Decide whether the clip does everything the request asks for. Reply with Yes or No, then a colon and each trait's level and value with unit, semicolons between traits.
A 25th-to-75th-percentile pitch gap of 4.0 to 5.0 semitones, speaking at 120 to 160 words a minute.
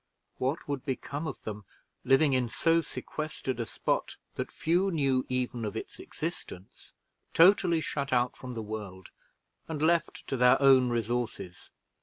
Yes: average, 4.6 semitones; average, 150 wpm